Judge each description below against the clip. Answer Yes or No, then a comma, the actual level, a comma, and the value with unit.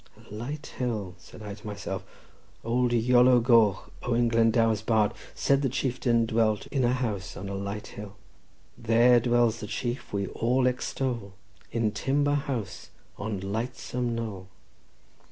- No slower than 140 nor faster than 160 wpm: Yes, average, 145 wpm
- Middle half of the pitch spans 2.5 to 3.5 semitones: Yes, average, 2.8 semitones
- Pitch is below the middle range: Yes, low, 115 Hz